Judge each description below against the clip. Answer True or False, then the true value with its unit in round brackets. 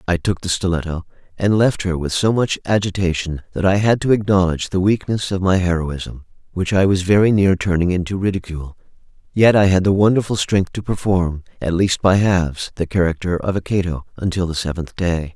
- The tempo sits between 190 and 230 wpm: True (195 wpm)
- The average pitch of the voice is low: True (90 Hz)